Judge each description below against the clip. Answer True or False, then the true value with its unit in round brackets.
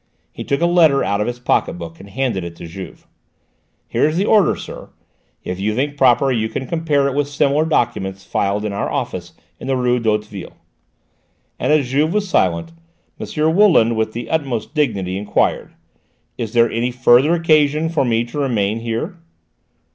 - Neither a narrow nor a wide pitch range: False (5.9 semitones)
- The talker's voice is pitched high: False (125 Hz)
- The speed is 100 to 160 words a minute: False (180 wpm)